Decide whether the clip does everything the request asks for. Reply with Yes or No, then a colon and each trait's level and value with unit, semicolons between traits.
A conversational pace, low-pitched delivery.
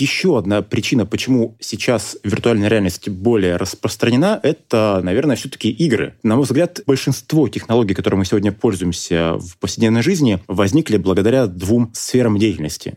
Yes: average, 140 wpm; low, 110 Hz